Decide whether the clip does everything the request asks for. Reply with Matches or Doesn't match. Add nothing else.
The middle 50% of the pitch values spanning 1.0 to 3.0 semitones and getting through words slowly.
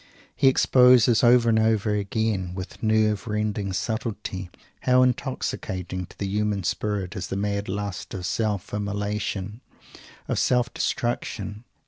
Matches